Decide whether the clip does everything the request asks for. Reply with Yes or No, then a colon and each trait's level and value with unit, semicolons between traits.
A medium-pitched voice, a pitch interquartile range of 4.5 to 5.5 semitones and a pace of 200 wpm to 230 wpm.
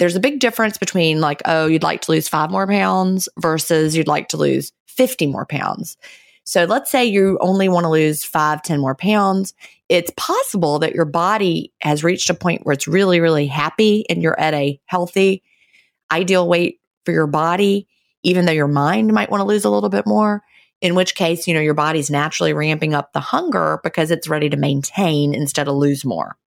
No: medium, 165 Hz; average, 4.0 semitones; fast, 205 wpm